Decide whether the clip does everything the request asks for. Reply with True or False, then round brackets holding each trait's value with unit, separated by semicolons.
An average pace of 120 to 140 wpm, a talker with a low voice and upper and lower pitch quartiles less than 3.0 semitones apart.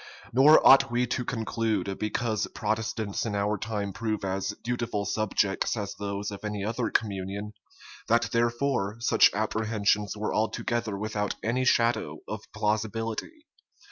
True (135 wpm; 110 Hz; 2.4 semitones)